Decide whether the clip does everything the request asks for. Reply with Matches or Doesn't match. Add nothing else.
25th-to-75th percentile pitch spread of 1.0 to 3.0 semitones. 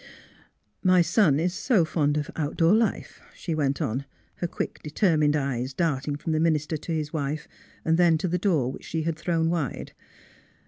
Matches